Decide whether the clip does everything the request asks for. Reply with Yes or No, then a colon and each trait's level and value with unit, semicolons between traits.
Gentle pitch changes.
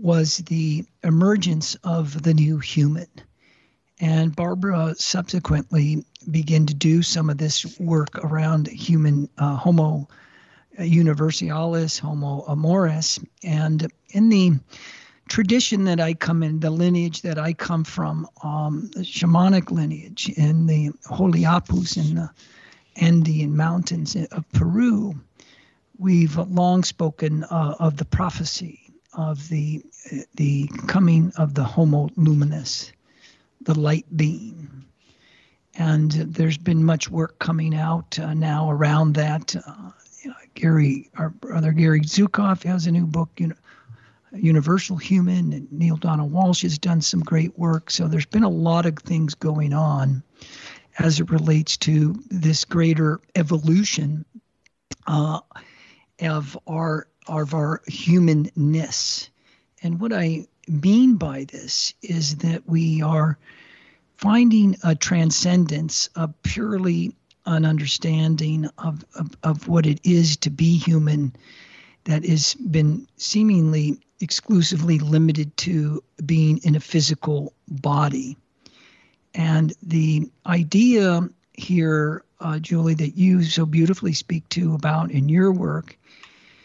Yes: narrow, 2.1 semitones